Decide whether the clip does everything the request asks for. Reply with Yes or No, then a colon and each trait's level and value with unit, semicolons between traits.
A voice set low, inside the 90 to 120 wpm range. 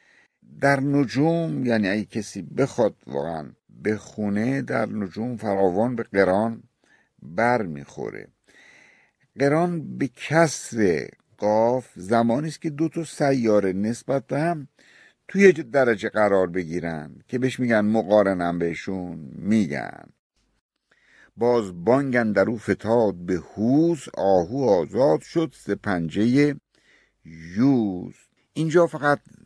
Yes: low, 115 Hz; average, 110 wpm